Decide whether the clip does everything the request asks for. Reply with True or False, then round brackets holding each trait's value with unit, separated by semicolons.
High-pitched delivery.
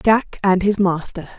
True (195 Hz)